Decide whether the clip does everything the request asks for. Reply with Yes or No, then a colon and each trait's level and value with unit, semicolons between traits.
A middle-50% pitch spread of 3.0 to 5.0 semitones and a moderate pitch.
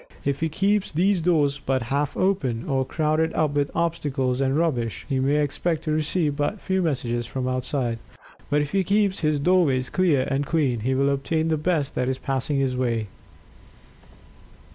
Yes: average, 3.7 semitones; medium, 145 Hz